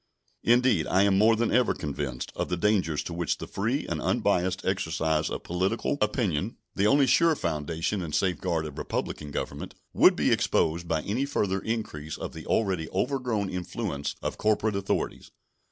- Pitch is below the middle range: Yes, very low, 95 Hz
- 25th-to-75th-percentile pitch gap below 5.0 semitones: No, average, 5.3 semitones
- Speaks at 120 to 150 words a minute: No, average, 170 wpm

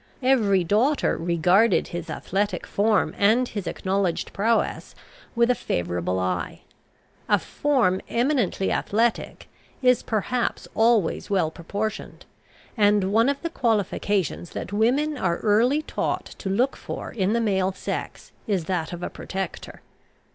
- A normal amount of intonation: Yes, average, 4.2 semitones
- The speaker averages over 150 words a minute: No, slow, 135 wpm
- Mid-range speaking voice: No, high, 205 Hz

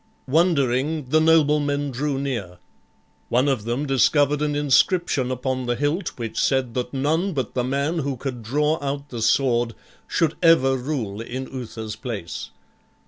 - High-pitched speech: No, low, 135 Hz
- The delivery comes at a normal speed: Yes, average, 150 wpm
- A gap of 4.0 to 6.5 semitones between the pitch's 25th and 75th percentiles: No, average, 3.2 semitones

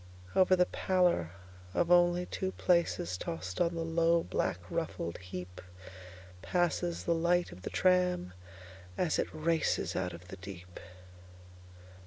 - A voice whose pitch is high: No, medium, 165 Hz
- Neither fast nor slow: No, slow, 120 wpm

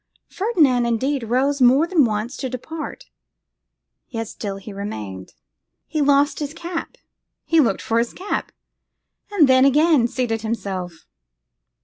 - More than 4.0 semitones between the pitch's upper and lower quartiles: Yes, average, 4.8 semitones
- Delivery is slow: Yes, slow, 130 wpm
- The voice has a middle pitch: No, very high, 255 Hz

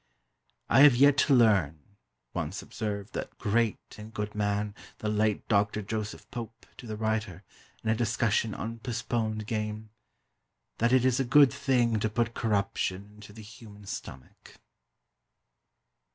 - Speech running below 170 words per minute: Yes, average, 145 wpm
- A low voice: Yes, low, 110 Hz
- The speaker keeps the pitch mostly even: Yes, narrow, 2.2 semitones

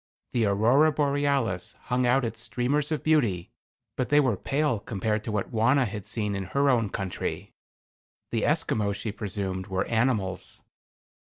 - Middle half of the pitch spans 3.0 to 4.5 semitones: No, average, 5.1 semitones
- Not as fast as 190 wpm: Yes, average, 155 wpm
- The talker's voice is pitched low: Yes, low, 115 Hz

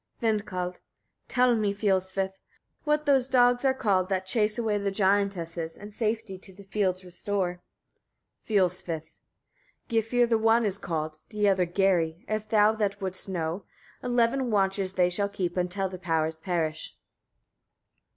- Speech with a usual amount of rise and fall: Yes, average, 3.2 semitones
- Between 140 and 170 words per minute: Yes, average, 150 wpm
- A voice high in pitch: Yes, high, 195 Hz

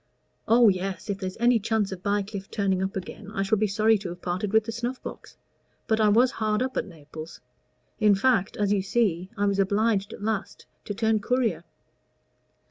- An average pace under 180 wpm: No, average, 200 wpm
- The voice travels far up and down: No, narrow, 2.5 semitones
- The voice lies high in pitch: Yes, high, 205 Hz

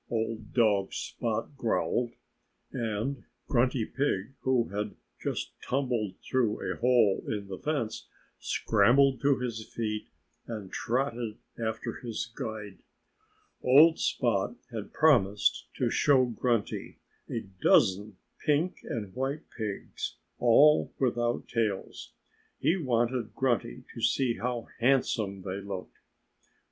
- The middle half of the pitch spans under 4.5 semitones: Yes, average, 3.4 semitones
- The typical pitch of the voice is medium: No, low, 115 Hz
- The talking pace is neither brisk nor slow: No, slow, 115 wpm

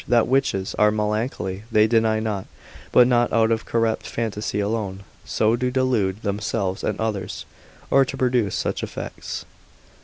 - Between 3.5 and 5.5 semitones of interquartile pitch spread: No, narrow, 2.5 semitones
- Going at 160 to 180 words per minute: No, average, 150 wpm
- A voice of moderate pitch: No, low, 110 Hz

